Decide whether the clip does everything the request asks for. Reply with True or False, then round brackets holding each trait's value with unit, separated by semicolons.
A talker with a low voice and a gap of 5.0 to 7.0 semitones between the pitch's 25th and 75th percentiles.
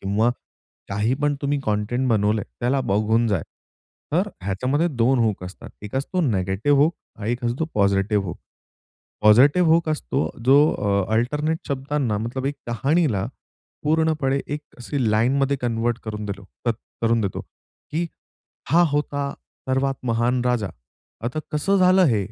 True (125 Hz; 5.3 semitones)